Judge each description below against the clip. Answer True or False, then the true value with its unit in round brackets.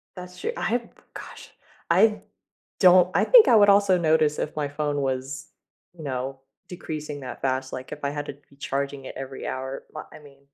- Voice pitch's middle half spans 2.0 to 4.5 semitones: False (4.9 semitones)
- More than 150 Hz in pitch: False (145 Hz)